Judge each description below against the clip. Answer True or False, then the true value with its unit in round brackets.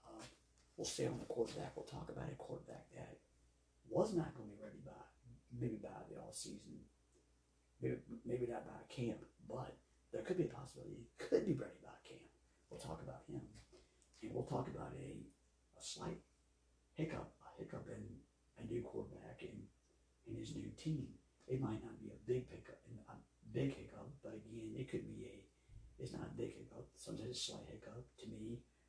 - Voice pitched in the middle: False (105 Hz)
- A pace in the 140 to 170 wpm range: False (190 wpm)